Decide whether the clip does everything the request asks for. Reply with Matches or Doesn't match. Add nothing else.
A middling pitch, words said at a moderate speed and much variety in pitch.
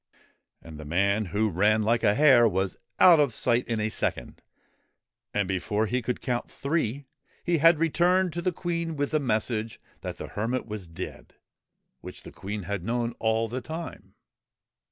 Doesn't match